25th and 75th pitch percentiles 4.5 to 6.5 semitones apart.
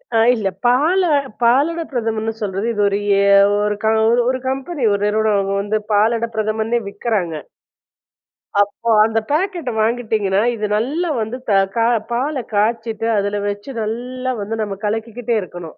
No: average, 2.9 semitones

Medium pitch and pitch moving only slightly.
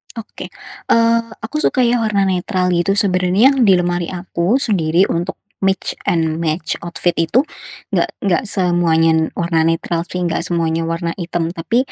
No: medium, 175 Hz; average, 3.1 semitones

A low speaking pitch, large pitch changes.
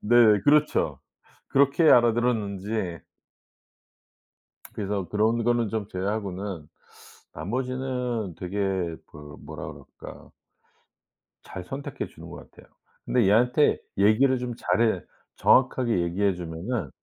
No: low, 110 Hz; average, 4.5 semitones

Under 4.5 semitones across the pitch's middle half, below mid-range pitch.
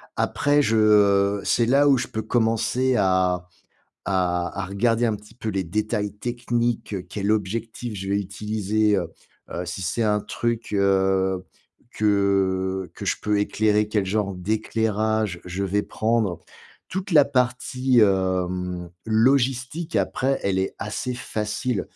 Yes: average, 3.5 semitones; low, 105 Hz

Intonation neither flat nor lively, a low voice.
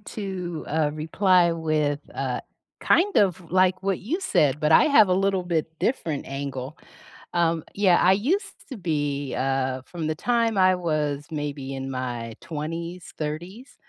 No: average, 4.6 semitones; medium, 165 Hz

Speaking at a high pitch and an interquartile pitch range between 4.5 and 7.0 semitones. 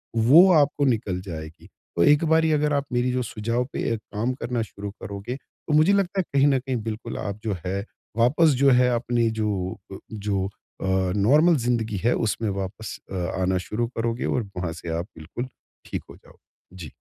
No: low, 115 Hz; wide, 5.4 semitones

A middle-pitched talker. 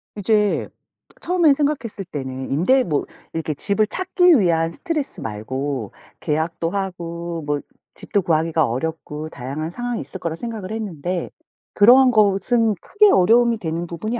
Yes: medium, 180 Hz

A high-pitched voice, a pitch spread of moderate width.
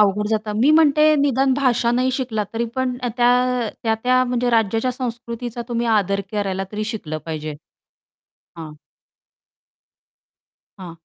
Yes: high, 235 Hz; average, 3.3 semitones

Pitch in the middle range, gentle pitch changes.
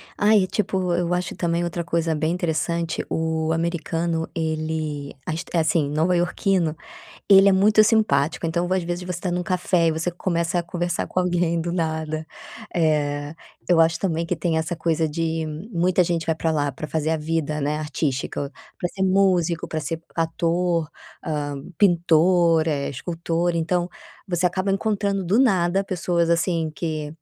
Yes: medium, 170 Hz; narrow, 2.0 semitones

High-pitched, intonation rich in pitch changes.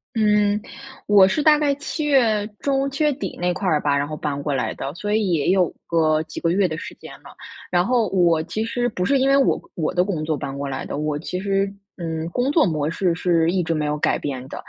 No: medium, 180 Hz; wide, 5.8 semitones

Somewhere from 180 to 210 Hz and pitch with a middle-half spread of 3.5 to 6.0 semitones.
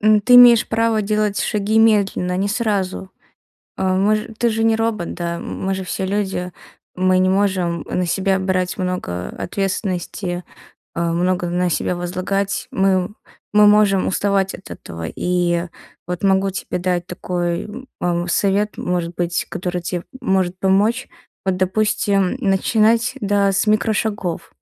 No: high, 190 Hz; narrow, 2.6 semitones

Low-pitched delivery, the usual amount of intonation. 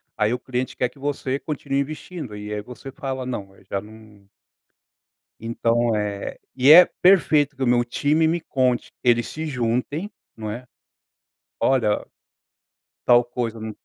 Yes: low, 125 Hz; average, 4.0 semitones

